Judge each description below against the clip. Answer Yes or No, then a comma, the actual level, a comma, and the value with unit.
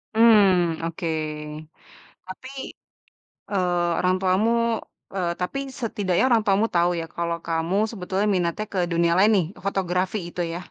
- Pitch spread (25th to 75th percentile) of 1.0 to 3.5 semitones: Yes, average, 2.7 semitones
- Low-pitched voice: No, medium, 185 Hz